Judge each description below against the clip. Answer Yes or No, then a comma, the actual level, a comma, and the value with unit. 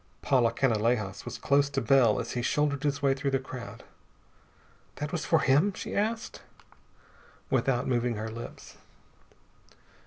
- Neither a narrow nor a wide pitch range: Yes, average, 3.3 semitones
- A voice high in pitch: No, low, 135 Hz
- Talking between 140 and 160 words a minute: Yes, average, 145 wpm